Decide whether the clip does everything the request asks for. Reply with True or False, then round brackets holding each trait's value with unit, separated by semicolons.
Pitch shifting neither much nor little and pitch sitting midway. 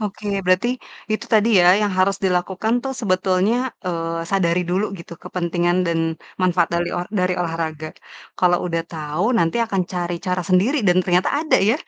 False (2.2 semitones; 180 Hz)